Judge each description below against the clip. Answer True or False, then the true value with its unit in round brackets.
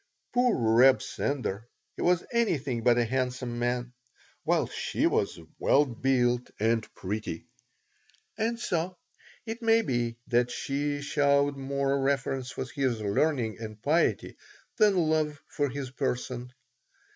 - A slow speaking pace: True (130 wpm)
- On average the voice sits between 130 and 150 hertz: True (135 Hz)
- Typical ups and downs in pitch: True (3.5 semitones)